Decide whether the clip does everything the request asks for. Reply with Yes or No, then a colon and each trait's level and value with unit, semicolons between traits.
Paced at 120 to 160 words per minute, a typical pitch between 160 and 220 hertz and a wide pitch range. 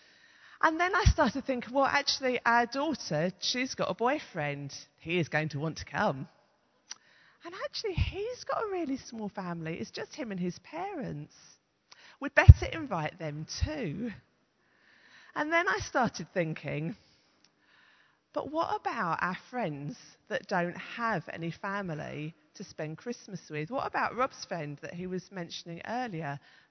Yes: average, 150 wpm; medium, 185 Hz; wide, 8.4 semitones